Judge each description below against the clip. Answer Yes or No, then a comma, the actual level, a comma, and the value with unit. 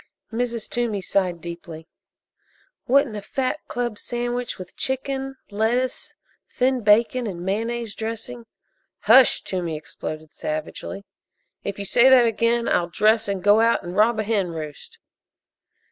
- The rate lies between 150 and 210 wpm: No, average, 140 wpm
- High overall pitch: Yes, high, 220 Hz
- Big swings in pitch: No, average, 4.1 semitones